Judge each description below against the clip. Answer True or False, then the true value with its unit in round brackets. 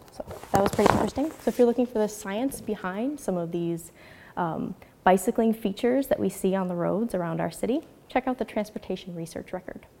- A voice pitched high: True (215 Hz)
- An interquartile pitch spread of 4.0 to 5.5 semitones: True (4.7 semitones)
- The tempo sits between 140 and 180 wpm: False (200 wpm)